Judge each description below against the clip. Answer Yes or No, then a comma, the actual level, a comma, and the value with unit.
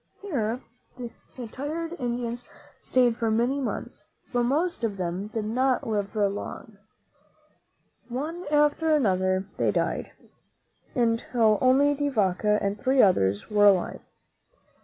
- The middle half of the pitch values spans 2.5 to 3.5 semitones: No, average, 4.7 semitones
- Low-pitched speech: No, high, 235 Hz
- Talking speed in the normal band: No, slow, 120 wpm